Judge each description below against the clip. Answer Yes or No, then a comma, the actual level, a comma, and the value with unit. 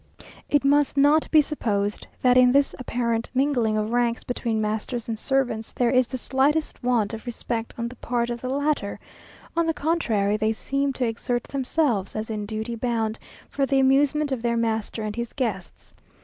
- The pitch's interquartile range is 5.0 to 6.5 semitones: No, average, 3.6 semitones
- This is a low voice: No, high, 240 Hz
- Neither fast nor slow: Yes, average, 185 wpm